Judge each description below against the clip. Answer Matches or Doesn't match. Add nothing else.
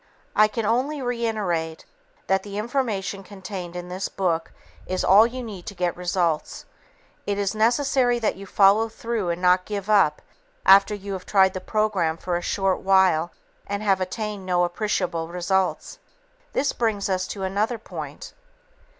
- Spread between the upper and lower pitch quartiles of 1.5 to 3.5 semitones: Matches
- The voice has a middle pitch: Doesn't match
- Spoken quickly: Doesn't match